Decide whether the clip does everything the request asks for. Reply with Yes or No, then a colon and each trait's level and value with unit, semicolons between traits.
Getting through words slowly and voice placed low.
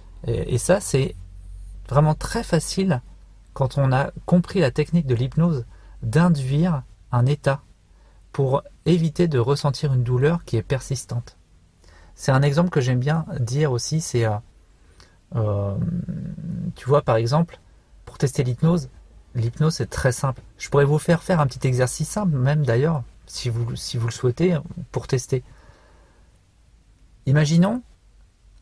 Yes: slow, 140 wpm; low, 130 Hz